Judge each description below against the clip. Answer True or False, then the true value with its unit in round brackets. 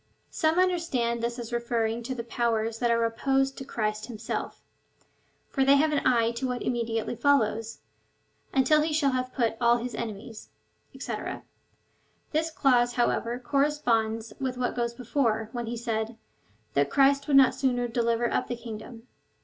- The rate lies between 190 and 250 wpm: False (160 wpm)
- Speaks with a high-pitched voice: True (240 Hz)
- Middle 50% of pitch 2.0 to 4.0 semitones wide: True (2.8 semitones)